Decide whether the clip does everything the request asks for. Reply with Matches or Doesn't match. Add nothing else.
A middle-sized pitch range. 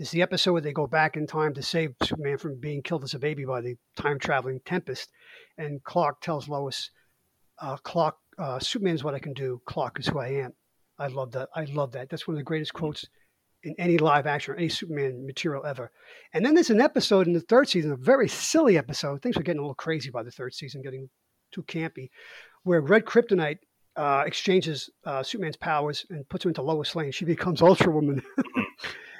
Matches